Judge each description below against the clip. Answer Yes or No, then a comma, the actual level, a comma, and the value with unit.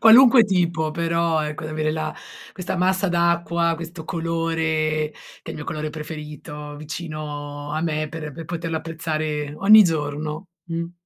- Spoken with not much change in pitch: Yes, narrow, 1.8 semitones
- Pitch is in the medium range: Yes, medium, 160 Hz